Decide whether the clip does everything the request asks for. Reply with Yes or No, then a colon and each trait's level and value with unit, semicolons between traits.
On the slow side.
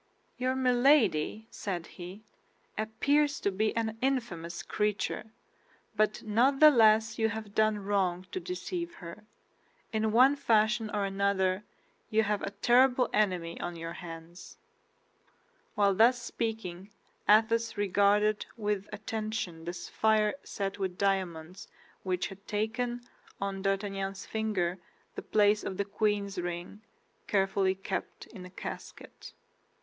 Yes: slow, 125 wpm